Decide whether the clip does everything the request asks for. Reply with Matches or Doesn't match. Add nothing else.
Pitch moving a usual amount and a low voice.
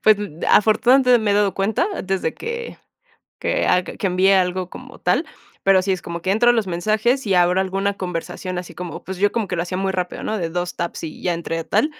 Doesn't match